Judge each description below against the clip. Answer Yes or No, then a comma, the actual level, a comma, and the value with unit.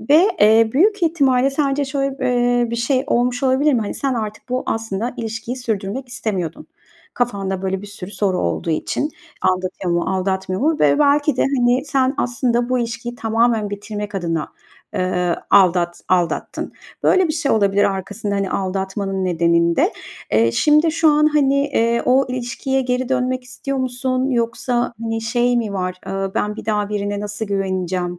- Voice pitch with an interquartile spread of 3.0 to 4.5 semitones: No, average, 4.9 semitones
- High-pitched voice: Yes, high, 230 Hz